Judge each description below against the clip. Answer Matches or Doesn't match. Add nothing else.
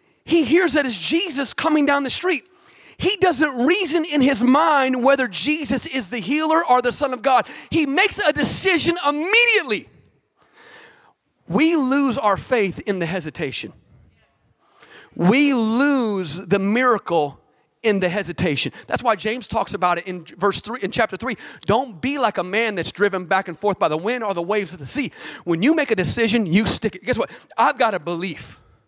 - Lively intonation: Matches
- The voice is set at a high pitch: Matches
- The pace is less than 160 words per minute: Doesn't match